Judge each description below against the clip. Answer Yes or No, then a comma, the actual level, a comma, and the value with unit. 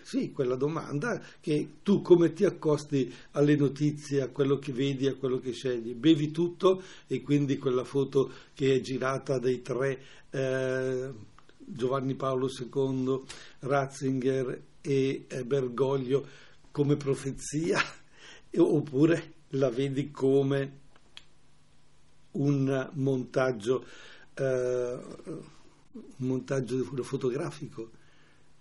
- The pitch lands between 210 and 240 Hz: No, low, 135 Hz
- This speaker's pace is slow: Yes, slow, 105 wpm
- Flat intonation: Yes, narrow, 1.7 semitones